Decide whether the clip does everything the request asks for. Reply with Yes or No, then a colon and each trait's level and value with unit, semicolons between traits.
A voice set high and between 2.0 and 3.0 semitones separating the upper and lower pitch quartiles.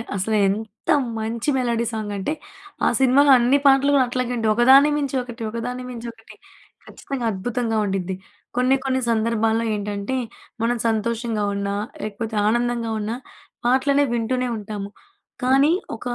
Yes: high, 235 Hz; average, 2.7 semitones